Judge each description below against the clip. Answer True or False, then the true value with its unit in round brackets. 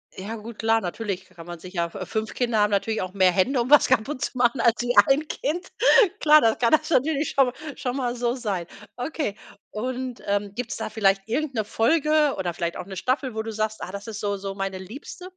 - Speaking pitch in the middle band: False (225 Hz)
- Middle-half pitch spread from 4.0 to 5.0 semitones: True (4.6 semitones)